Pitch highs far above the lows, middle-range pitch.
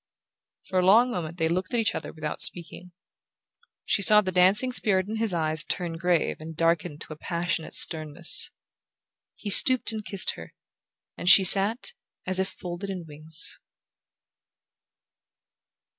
No: average, 3.6 semitones; medium, 180 Hz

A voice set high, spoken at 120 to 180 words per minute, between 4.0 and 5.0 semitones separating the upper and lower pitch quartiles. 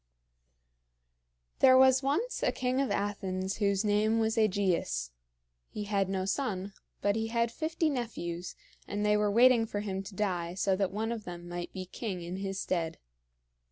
No: high, 205 Hz; average, 170 wpm; average, 3.3 semitones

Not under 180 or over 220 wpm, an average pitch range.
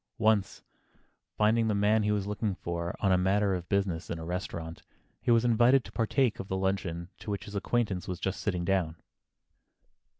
Yes: average, 190 wpm; average, 3.0 semitones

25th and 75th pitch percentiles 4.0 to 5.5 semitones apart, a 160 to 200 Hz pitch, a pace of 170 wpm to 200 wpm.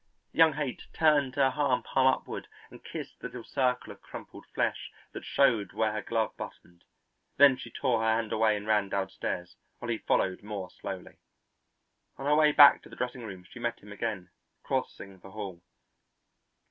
No: average, 4.8 semitones; low, 115 Hz; average, 180 wpm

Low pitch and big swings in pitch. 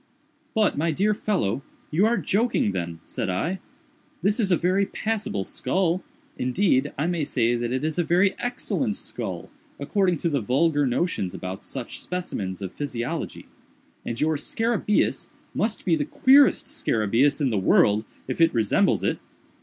No: medium, 160 Hz; wide, 8.8 semitones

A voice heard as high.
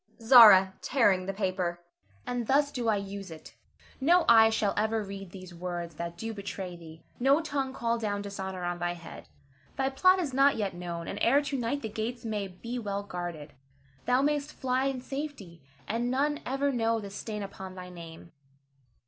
Yes: high, 215 Hz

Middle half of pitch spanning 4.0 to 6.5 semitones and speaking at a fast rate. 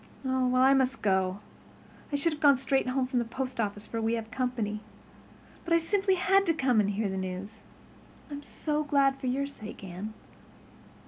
No: average, 4.6 semitones; average, 190 wpm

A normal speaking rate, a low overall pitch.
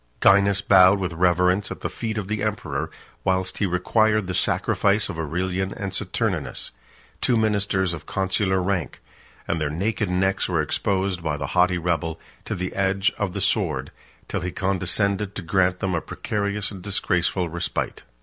Yes: average, 170 wpm; very low, 95 Hz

